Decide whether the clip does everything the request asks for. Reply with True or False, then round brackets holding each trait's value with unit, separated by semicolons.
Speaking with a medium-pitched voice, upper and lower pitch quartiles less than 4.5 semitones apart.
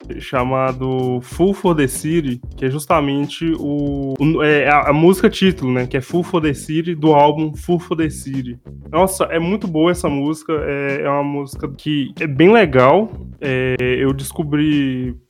True (145 Hz; 3.7 semitones)